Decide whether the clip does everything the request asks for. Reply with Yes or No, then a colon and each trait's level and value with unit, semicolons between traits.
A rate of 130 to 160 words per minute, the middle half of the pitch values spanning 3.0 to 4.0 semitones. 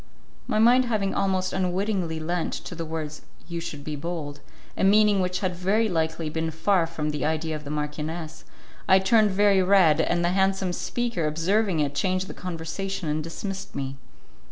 No: average, 180 wpm; average, 3.5 semitones